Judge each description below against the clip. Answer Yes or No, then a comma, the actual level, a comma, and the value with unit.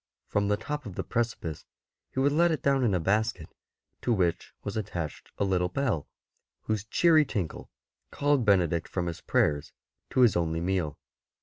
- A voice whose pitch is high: No, low, 100 Hz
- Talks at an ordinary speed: Yes, average, 175 wpm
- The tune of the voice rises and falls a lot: Yes, wide, 6.5 semitones